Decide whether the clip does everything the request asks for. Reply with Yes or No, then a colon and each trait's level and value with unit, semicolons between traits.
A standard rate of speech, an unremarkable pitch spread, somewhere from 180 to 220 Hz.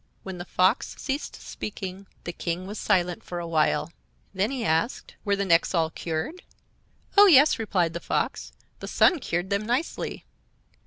Yes: average, 165 wpm; average, 4.9 semitones; high, 190 Hz